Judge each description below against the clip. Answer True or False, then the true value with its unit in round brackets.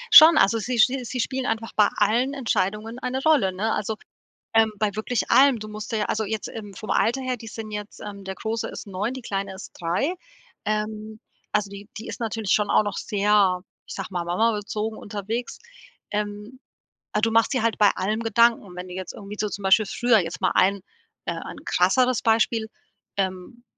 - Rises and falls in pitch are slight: True (2.3 semitones)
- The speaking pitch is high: True (215 Hz)